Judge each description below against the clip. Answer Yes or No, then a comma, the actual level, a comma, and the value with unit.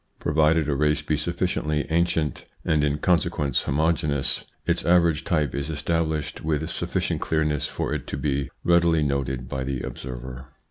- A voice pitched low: Yes, very low, 75 Hz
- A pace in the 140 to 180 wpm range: Yes, average, 155 wpm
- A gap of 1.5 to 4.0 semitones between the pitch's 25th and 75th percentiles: Yes, average, 2.7 semitones